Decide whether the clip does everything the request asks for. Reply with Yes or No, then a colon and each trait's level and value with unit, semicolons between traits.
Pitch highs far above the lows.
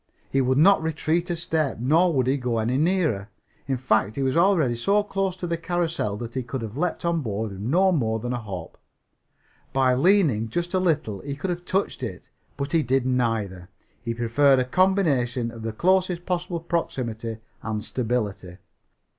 Yes: wide, 6.8 semitones